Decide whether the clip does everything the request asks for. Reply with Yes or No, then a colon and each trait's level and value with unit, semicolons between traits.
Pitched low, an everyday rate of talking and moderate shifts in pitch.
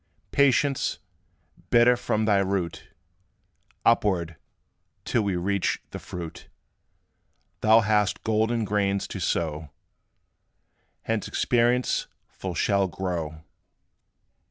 No: low, 100 Hz; slow, 90 wpm; average, 4.2 semitones